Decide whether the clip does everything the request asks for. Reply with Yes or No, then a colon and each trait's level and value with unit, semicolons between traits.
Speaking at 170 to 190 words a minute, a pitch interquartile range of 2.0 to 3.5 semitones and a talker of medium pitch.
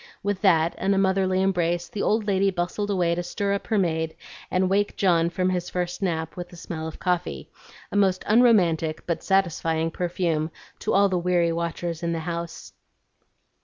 Yes: average, 185 wpm; narrow, 2.5 semitones; medium, 180 Hz